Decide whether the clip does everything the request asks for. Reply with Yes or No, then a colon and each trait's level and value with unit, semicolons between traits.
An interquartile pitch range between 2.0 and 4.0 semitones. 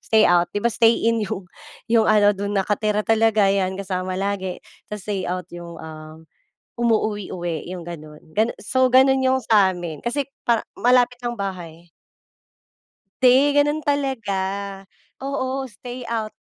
No: average, 4.5 semitones